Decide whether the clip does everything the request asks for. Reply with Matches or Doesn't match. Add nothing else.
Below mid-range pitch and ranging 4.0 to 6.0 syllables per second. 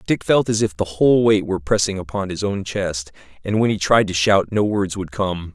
Matches